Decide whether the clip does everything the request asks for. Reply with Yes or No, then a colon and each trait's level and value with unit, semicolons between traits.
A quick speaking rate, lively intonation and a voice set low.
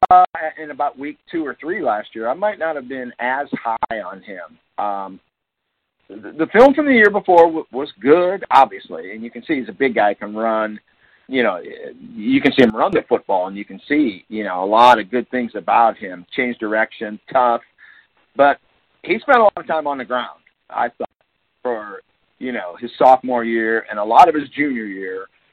Yes: fast, 210 wpm; wide, 7.0 semitones; low, 130 Hz